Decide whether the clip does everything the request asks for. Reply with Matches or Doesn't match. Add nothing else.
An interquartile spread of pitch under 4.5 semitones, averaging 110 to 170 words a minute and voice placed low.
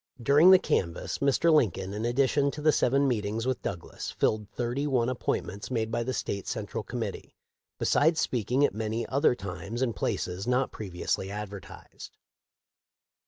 Doesn't match